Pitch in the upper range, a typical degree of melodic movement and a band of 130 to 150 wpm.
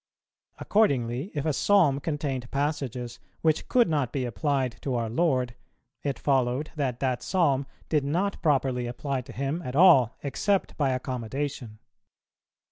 No: low, 135 Hz; average, 3.3 semitones; average, 140 wpm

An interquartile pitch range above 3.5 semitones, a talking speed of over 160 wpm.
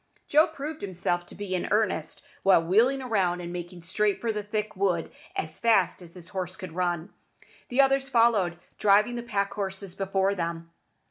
Yes: average, 3.9 semitones; average, 180 wpm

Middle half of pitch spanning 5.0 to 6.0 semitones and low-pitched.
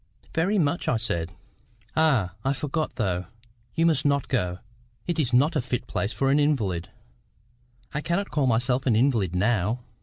Yes: wide, 5.6 semitones; low, 130 Hz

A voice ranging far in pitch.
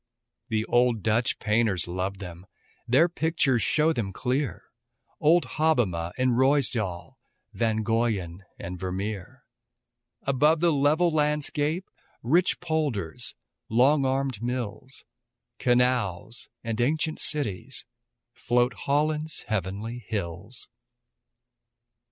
Yes: wide, 6.0 semitones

